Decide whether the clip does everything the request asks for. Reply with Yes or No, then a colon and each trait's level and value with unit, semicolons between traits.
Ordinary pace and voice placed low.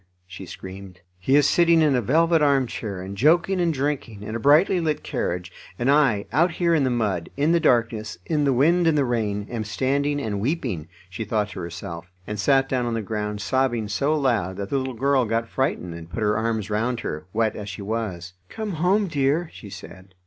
No: fast, 215 wpm; low, 115 Hz